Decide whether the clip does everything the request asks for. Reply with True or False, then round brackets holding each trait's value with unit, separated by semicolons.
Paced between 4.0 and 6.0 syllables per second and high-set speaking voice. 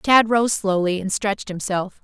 True (4.5 syllables/s; 200 Hz)